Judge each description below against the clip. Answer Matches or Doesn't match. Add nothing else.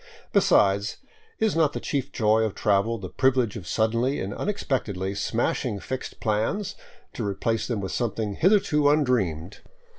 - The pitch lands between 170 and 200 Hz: Doesn't match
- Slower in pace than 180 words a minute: Matches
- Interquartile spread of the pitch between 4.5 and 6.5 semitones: Matches